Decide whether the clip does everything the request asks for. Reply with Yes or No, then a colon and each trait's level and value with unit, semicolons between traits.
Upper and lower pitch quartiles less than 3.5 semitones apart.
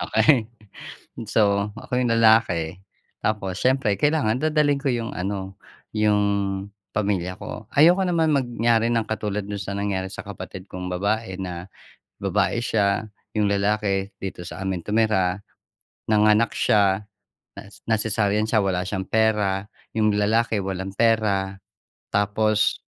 Yes: narrow, 2.4 semitones